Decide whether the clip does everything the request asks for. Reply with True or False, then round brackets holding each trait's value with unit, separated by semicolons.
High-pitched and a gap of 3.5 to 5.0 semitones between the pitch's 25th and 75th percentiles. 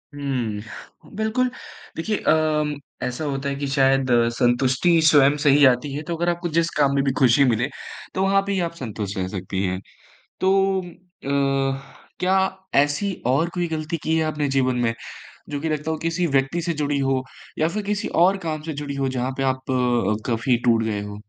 False (140 Hz; 4.1 semitones)